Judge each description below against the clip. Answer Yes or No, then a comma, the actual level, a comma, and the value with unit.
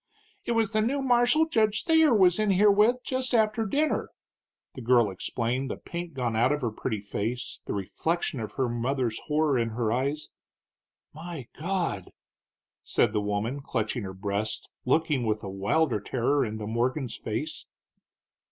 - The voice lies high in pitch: No, low, 135 Hz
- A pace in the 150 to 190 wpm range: Yes, average, 160 wpm